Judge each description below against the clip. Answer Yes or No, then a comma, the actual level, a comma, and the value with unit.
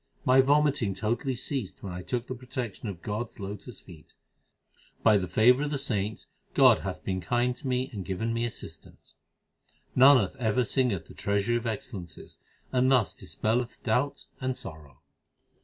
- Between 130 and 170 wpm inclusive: Yes, average, 165 wpm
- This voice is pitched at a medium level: No, low, 115 Hz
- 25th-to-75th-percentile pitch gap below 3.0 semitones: No, average, 4.1 semitones